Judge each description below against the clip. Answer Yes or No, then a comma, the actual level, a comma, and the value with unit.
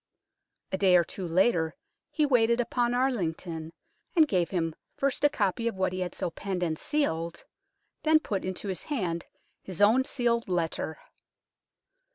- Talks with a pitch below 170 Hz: No, high, 190 Hz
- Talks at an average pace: Yes, average, 160 wpm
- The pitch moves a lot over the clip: Yes, wide, 6.0 semitones